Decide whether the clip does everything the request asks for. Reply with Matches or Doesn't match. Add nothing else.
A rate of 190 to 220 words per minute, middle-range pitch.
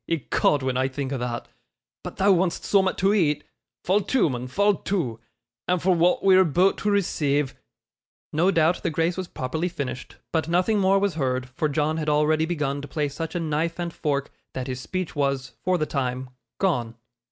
Matches